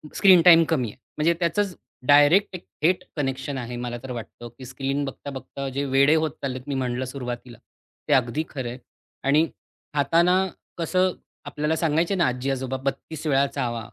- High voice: No, medium, 140 Hz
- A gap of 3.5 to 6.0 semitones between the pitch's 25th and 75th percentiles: Yes, average, 3.8 semitones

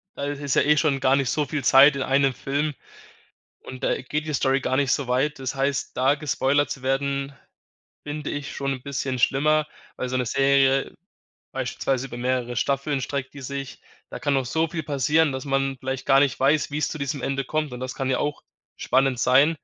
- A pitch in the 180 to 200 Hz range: No, low, 135 Hz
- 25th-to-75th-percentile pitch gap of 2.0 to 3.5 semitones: No, narrow, 1.6 semitones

